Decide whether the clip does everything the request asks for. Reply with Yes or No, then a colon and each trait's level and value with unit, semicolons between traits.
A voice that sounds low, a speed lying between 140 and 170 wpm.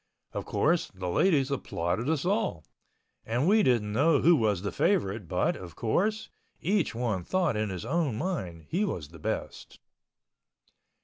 Yes: low, 125 Hz; average, 150 wpm